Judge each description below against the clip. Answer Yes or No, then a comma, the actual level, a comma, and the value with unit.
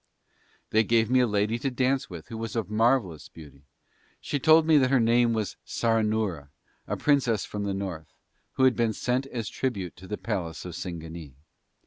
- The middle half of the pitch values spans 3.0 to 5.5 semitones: Yes, average, 5.2 semitones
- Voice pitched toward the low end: Yes, low, 110 Hz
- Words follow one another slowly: No, average, 185 wpm